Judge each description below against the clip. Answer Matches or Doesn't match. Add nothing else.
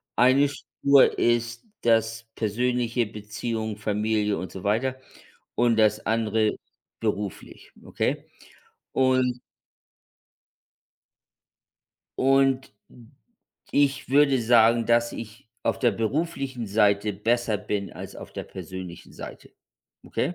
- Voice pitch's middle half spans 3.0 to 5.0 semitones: Matches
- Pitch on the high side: Doesn't match